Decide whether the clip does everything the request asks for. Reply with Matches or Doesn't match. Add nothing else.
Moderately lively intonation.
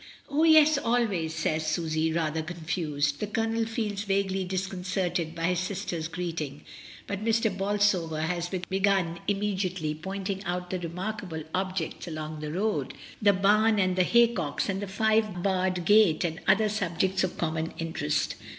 Matches